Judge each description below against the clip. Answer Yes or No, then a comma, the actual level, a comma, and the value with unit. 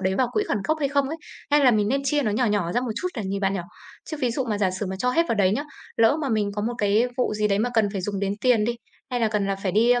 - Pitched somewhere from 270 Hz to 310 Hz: No, high, 220 Hz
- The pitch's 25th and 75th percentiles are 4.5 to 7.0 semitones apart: No, average, 3.8 semitones